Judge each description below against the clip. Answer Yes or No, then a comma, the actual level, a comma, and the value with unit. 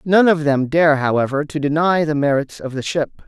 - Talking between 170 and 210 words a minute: No, fast, 220 wpm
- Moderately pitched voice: Yes, medium, 150 Hz